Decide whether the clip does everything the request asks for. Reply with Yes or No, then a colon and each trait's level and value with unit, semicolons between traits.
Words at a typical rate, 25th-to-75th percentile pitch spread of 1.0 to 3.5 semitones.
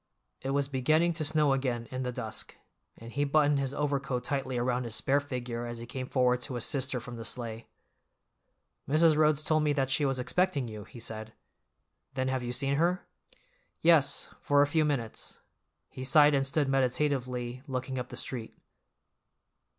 Yes: average, 180 wpm; average, 2.8 semitones